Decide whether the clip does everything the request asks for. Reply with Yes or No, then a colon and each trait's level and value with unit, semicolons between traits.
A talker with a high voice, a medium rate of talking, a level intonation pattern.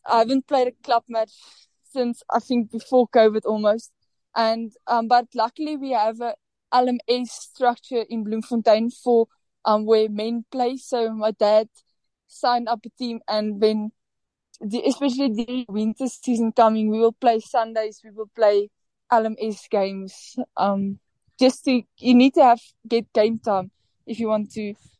Yes: high, 230 Hz; average, 160 wpm; narrow, 2.1 semitones